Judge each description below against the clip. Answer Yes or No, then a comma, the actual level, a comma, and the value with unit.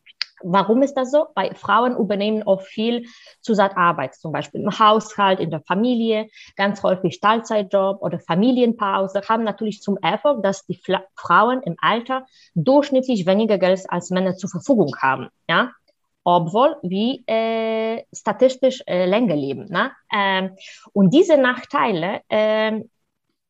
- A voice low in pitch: No, high, 210 Hz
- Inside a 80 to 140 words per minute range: Yes, average, 135 wpm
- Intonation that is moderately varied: Yes, average, 3.2 semitones